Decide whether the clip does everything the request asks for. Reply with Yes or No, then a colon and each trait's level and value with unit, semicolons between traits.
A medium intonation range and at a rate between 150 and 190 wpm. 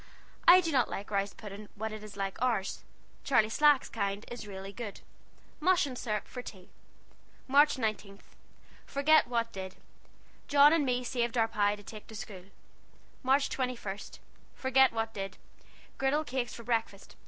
Yes: average, 4.5 semitones; average, 160 wpm